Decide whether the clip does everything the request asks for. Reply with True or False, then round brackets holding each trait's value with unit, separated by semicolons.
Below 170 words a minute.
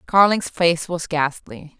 True (135 wpm)